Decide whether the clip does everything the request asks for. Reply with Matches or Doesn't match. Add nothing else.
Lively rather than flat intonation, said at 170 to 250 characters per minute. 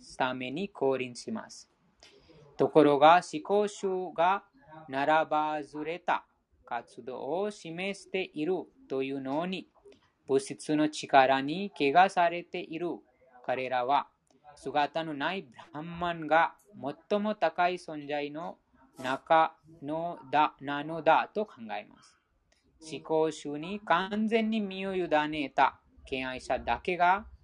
Doesn't match